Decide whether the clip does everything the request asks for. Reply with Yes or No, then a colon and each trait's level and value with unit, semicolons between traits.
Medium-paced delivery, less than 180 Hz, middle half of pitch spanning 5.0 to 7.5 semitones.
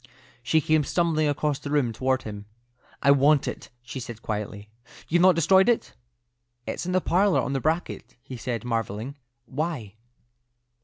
Yes: average, 160 wpm; medium, 140 Hz; average, 5.3 semitones